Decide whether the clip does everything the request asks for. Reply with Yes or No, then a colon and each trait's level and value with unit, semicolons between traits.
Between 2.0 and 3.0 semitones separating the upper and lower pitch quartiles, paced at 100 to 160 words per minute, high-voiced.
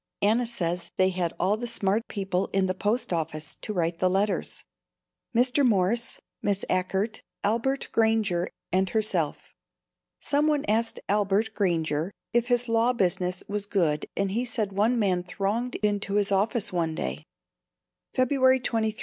No: average, 3.9 semitones; average, 150 wpm; high, 205 Hz